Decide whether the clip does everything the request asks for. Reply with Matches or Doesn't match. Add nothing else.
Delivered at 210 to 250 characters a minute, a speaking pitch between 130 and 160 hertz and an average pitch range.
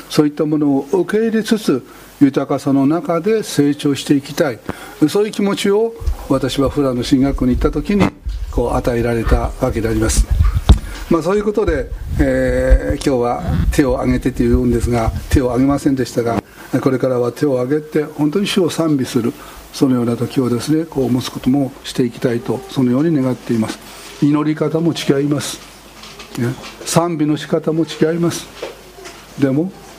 Doesn't match